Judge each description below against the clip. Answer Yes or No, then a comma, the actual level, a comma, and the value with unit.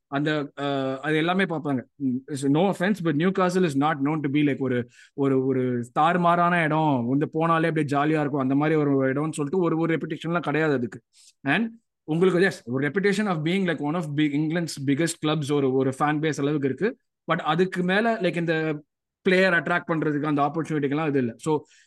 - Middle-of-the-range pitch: Yes, medium, 155 Hz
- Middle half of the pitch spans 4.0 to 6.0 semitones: No, average, 3.4 semitones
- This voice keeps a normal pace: No, fast, 170 wpm